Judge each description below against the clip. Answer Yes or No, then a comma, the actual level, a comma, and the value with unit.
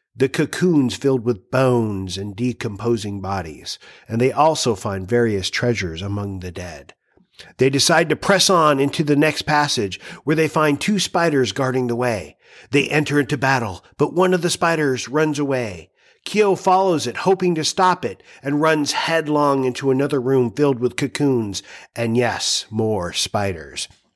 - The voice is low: Yes, low, 130 Hz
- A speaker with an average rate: Yes, average, 160 wpm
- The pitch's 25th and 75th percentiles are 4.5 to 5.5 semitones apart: Yes, average, 5.1 semitones